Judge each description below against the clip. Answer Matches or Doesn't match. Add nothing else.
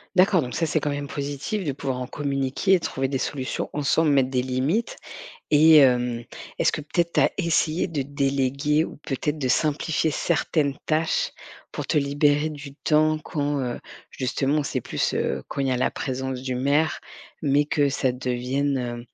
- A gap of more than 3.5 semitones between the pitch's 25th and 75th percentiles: Doesn't match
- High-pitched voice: Doesn't match